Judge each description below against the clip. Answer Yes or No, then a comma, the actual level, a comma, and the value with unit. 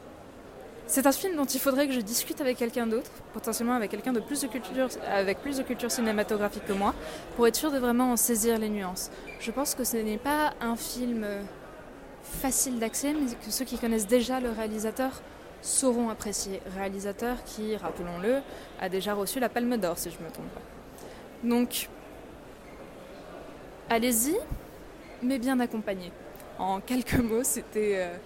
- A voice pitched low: No, high, 235 Hz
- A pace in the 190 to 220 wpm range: No, average, 170 wpm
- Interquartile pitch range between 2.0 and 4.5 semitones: Yes, average, 3.3 semitones